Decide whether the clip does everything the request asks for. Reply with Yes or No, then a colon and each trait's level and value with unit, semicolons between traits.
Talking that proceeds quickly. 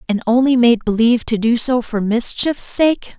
No: average, 190 wpm